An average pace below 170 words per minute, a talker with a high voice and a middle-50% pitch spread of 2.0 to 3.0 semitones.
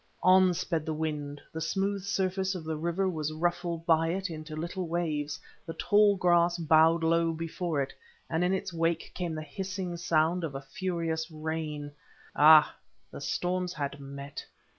No: average, 160 wpm; medium, 165 Hz; narrow, 2.5 semitones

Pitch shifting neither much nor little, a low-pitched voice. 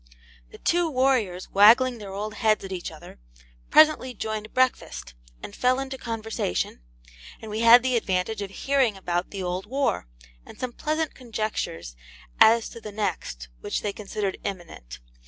No: average, 4.8 semitones; high, 215 Hz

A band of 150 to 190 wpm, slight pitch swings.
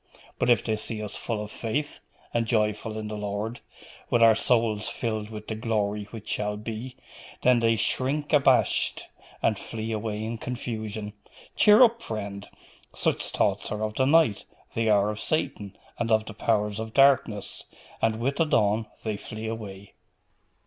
Yes: average, 170 wpm; narrow, 1.8 semitones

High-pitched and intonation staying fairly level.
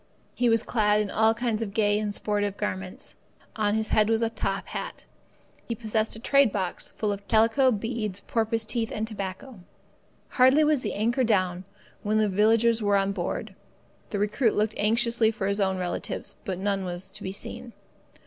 Yes: high, 215 Hz; narrow, 2.2 semitones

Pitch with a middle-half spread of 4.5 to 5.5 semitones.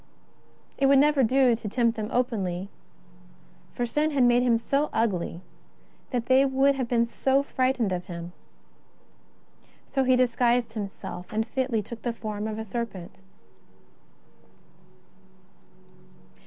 No: average, 3.5 semitones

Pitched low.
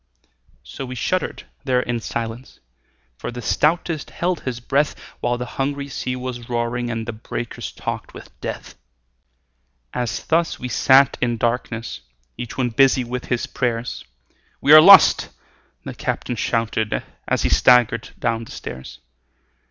Yes: low, 125 Hz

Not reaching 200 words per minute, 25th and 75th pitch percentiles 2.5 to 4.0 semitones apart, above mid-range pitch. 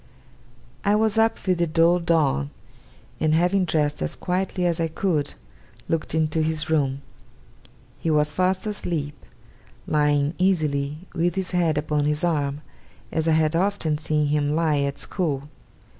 No: average, 150 wpm; average, 3.0 semitones; medium, 160 Hz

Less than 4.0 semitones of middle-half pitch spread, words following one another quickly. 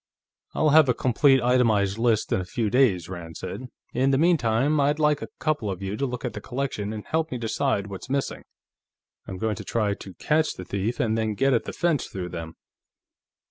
No: wide, 5.5 semitones; fast, 215 wpm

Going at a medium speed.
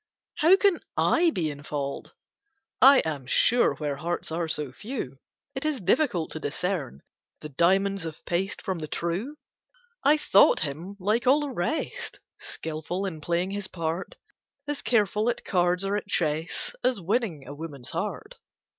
Yes: average, 160 wpm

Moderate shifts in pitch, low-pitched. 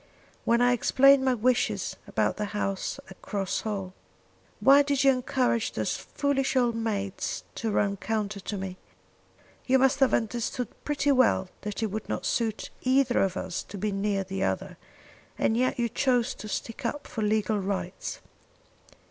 No: average, 4.2 semitones; high, 225 Hz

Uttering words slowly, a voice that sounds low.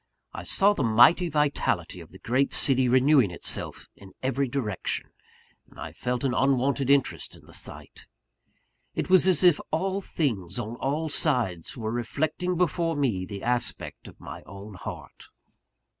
No: average, 160 wpm; low, 130 Hz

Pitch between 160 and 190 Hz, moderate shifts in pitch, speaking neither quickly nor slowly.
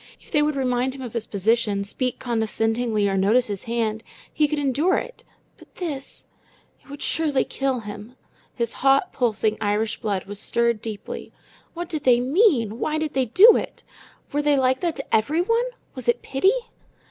No: very high, 250 Hz; average, 4.9 semitones; average, 180 wpm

